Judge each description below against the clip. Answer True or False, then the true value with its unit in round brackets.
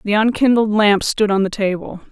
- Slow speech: False (200 wpm)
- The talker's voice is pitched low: False (205 Hz)